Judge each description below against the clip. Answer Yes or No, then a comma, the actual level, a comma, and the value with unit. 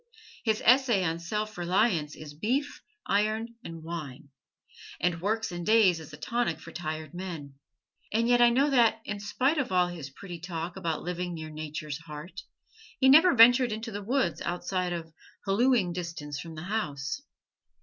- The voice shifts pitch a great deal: Yes, wide, 5.7 semitones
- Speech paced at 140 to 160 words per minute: No, average, 170 wpm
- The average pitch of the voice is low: No, medium, 180 Hz